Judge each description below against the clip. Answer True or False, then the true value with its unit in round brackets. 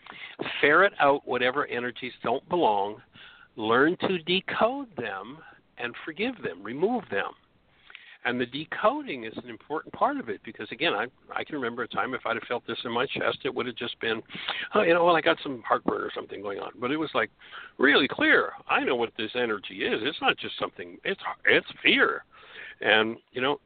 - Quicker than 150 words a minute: True (205 wpm)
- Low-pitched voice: False (190 Hz)